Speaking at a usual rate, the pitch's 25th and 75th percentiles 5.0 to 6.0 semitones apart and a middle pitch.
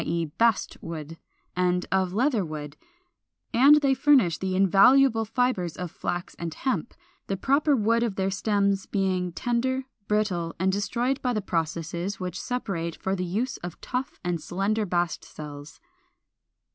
No: average, 145 wpm; average, 5.3 semitones; high, 195 Hz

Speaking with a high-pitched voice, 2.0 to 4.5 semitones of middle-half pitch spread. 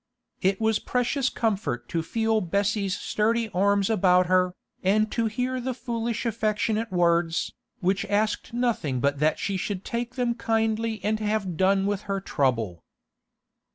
Yes: high, 210 Hz; average, 3.7 semitones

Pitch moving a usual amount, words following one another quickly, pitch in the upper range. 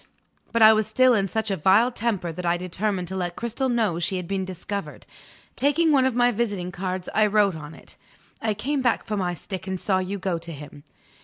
Yes: average, 3.9 semitones; fast, 225 wpm; high, 195 Hz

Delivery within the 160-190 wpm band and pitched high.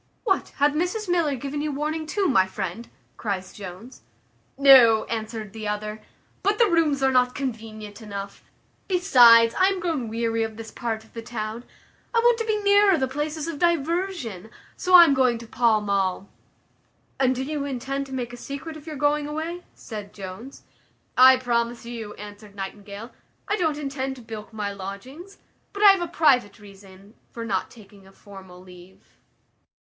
Yes: average, 175 wpm; high, 245 Hz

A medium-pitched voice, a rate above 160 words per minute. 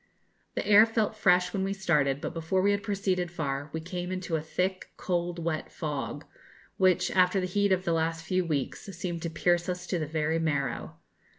Yes: medium, 175 Hz; average, 200 wpm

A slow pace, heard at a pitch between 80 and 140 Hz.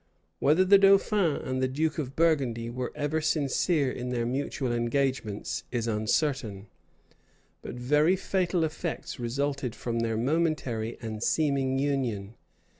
Yes: slow, 130 wpm; low, 135 Hz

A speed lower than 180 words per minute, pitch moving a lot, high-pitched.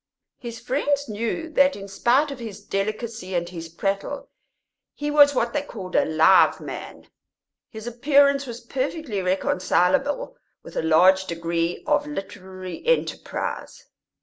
Yes: slow, 135 wpm; wide, 7.0 semitones; high, 225 Hz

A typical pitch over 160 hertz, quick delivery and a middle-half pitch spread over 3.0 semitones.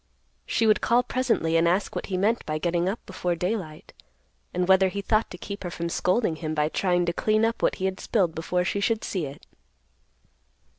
Yes: medium, 185 Hz; fast, 210 wpm; average, 3.8 semitones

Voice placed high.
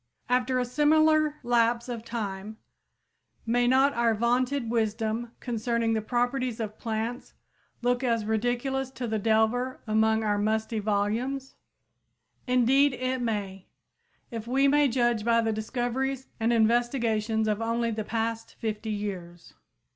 Yes: high, 235 Hz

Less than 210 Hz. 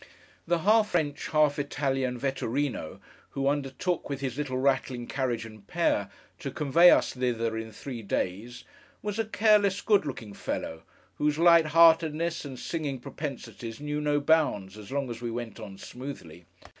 Yes: medium, 140 Hz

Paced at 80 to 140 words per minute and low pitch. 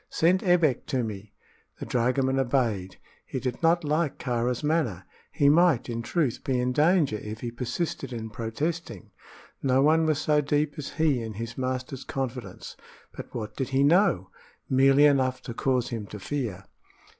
No: average, 165 wpm; low, 130 Hz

